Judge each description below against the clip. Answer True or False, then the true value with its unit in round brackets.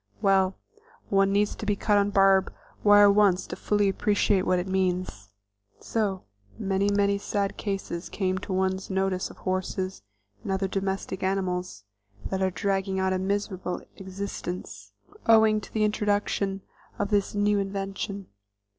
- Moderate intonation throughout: False (1.3 semitones)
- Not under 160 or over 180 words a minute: False (150 wpm)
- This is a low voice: False (195 Hz)